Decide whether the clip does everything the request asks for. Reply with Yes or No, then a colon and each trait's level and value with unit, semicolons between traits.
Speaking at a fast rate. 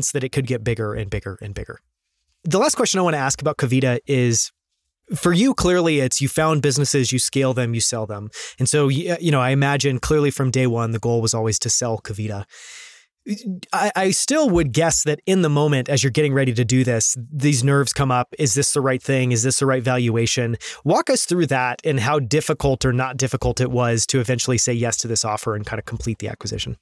Yes: fast, 230 wpm